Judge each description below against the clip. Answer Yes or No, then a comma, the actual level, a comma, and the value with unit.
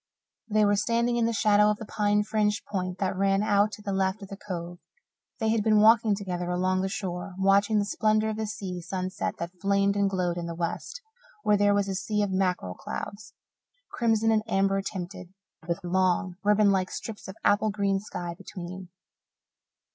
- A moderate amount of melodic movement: No, narrow, 2.3 semitones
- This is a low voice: No, high, 200 Hz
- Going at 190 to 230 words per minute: Yes, average, 195 wpm